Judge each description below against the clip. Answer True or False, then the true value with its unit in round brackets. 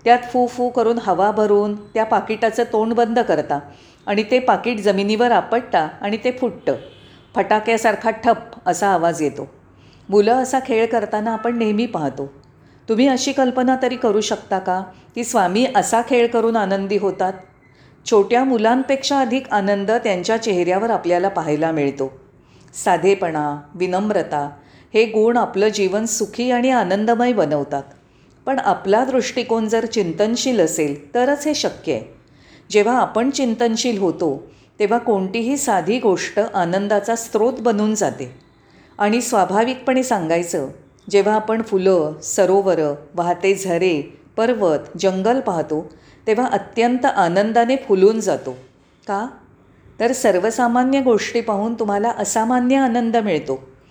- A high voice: True (215 Hz)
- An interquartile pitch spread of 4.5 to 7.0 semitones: False (4.1 semitones)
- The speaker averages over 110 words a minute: True (125 wpm)